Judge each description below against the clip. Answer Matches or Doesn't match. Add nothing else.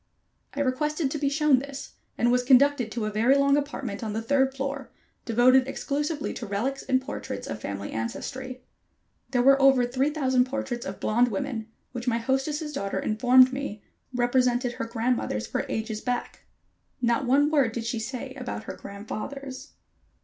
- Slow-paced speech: Doesn't match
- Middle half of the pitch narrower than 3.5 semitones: Matches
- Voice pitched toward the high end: Matches